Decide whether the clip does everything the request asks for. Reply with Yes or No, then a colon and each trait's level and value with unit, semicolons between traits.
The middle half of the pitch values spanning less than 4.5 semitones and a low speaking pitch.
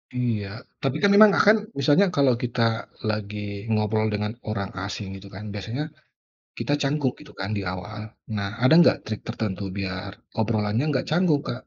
No: average, 5.1 semitones; low, 110 Hz